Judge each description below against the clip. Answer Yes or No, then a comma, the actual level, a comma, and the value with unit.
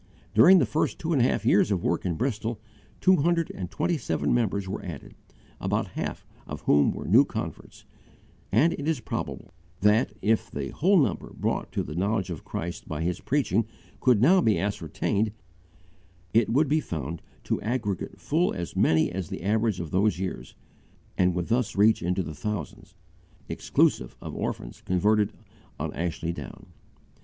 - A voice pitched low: Yes, low, 105 Hz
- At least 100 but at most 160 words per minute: No, average, 170 wpm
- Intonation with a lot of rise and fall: Yes, wide, 5.9 semitones